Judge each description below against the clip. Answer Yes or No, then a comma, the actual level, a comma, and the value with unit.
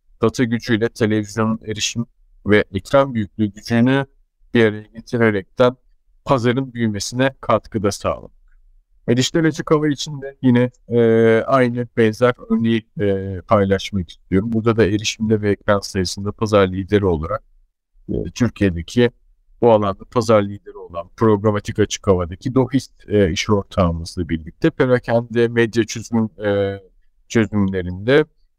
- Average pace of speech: Yes, average, 115 wpm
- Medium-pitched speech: No, low, 110 Hz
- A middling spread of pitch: Yes, average, 3.3 semitones